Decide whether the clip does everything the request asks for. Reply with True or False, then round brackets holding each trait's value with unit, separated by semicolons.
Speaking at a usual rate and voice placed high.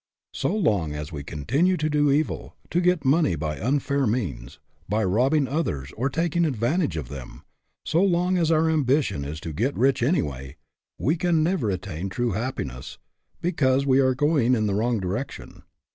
False (175 wpm; 130 Hz)